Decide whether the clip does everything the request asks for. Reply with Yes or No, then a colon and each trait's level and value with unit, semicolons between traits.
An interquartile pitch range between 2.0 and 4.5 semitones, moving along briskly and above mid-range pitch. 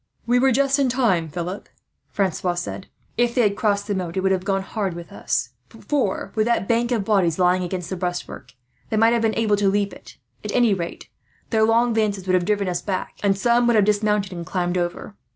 Yes: average, 3.8 semitones; fast, 225 wpm; high, 200 Hz